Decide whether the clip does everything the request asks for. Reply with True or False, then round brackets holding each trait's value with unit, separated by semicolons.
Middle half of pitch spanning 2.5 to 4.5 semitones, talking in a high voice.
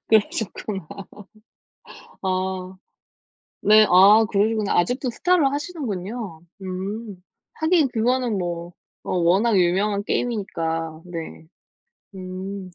True (3.6 semitones; 200 Hz)